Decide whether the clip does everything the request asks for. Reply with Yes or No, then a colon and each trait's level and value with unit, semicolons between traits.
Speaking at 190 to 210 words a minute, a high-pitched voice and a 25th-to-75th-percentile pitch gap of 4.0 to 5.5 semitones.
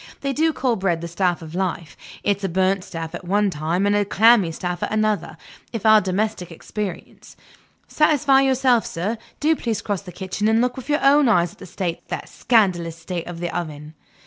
Yes: average, 200 wpm; high, 195 Hz; average, 4.8 semitones